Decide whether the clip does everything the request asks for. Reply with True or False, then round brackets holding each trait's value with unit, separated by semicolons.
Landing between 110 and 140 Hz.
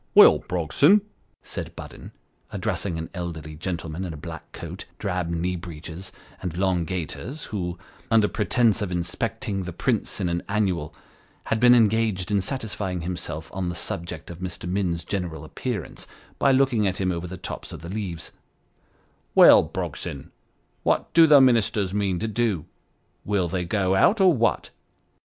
False (95 Hz)